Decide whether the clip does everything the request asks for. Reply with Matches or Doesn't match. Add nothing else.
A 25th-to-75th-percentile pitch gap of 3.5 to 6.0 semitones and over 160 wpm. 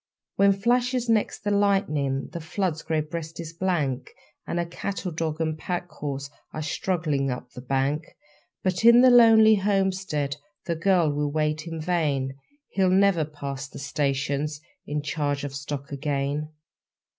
Doesn't match